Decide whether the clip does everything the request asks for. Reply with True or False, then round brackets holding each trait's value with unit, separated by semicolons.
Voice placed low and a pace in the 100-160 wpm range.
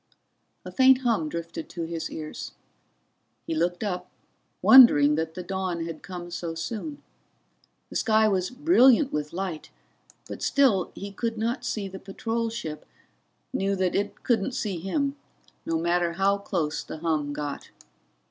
False (190 Hz; 150 wpm)